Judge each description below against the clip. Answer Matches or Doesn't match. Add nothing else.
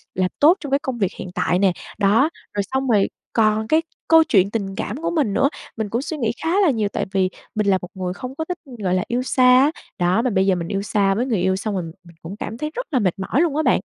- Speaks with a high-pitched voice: Matches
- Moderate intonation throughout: Doesn't match